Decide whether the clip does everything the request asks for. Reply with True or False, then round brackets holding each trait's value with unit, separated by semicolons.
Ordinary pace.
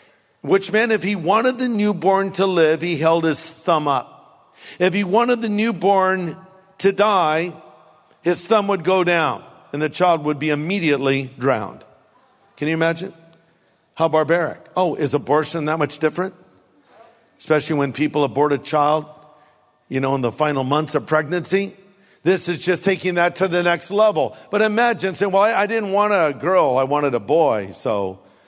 True (170 wpm)